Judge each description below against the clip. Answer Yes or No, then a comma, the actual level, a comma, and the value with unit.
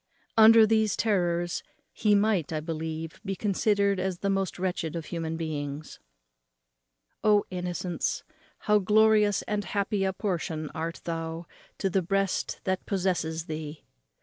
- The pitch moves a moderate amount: Yes, average, 3.9 semitones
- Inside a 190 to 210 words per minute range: No, slow, 135 wpm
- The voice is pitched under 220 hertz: Yes, medium, 185 Hz